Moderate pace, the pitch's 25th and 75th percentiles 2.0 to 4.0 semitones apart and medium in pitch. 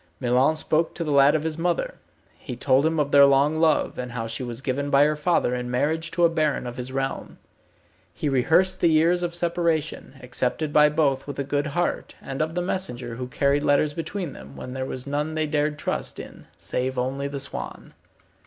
No: fast, 215 wpm; average, 3.3 semitones; medium, 145 Hz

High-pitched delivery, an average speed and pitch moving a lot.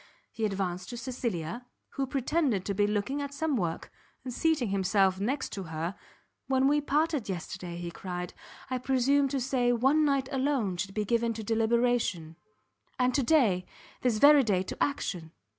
Yes: high, 235 Hz; average, 165 wpm; wide, 6.0 semitones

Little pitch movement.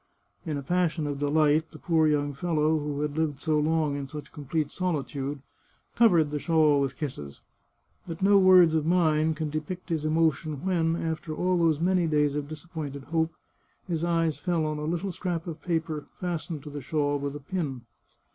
Yes: narrow, 2.2 semitones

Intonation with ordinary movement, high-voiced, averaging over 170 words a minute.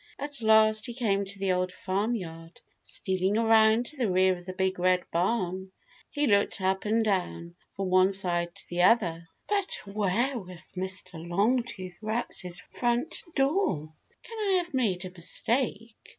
No: average, 4.2 semitones; high, 195 Hz; average, 165 wpm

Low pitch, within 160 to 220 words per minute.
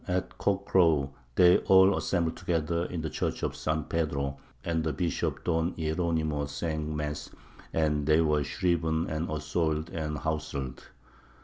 No: very low, 80 Hz; average, 145 wpm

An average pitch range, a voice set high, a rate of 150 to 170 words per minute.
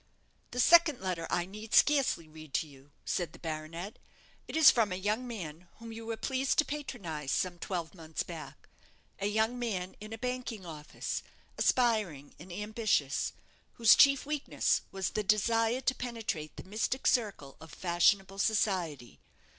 No: wide, 5.7 semitones; high, 205 Hz; average, 160 wpm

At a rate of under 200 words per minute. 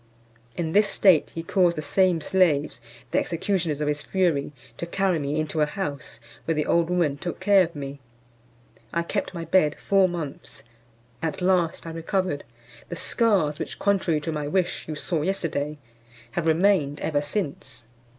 Yes: average, 170 wpm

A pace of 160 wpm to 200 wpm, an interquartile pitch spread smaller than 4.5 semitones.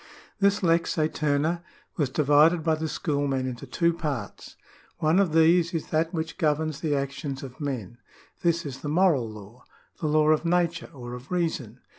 Yes: average, 175 wpm; average, 3.4 semitones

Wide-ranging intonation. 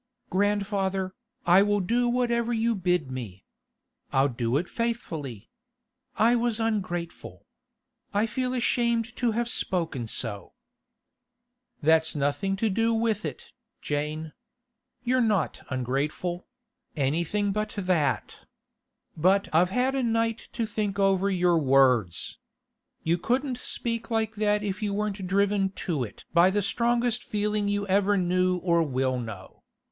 Yes: wide, 5.8 semitones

